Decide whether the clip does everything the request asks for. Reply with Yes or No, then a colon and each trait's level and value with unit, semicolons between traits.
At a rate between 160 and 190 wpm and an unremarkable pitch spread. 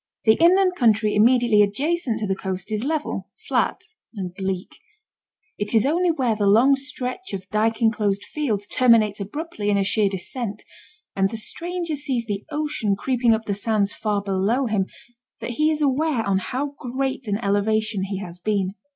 Yes: average, 175 wpm; average, 5.0 semitones